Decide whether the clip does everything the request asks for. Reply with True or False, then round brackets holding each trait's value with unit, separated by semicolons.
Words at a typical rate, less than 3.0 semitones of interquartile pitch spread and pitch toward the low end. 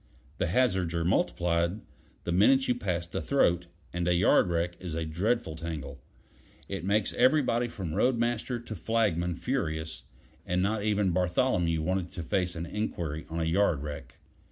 False (165 wpm; 4.6 semitones; 90 Hz)